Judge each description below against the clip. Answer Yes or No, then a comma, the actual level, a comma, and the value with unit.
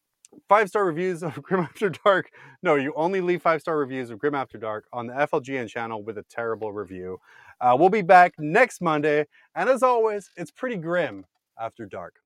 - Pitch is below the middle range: No, medium, 150 Hz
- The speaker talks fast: No, average, 195 wpm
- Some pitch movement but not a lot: No, wide, 7.5 semitones